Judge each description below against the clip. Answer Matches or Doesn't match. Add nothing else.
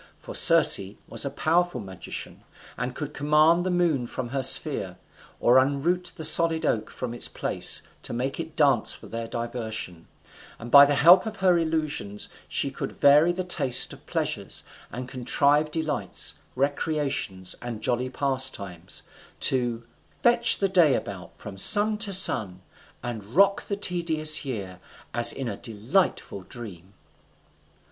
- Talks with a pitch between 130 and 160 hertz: Matches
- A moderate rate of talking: Matches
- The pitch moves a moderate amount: Doesn't match